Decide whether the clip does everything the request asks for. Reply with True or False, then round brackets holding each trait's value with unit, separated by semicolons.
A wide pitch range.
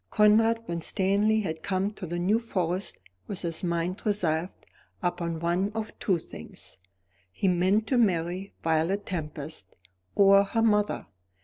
False (3.6 semitones)